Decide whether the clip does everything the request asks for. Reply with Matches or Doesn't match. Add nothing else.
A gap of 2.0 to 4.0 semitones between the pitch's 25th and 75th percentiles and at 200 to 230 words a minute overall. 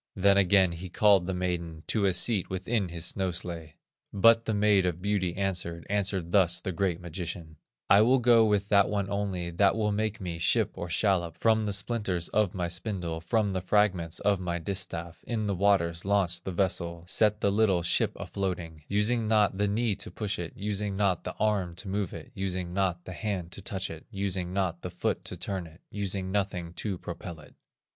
Matches